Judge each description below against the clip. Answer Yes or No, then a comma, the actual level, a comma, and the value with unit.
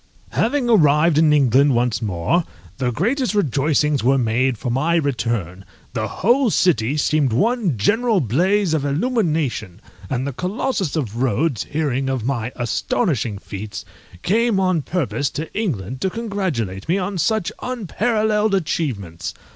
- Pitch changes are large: Yes, wide, 8.3 semitones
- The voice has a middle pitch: Yes, medium, 150 Hz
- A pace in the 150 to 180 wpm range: No, average, 140 wpm